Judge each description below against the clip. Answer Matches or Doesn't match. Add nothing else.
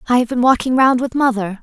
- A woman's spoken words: Matches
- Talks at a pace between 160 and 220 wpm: Doesn't match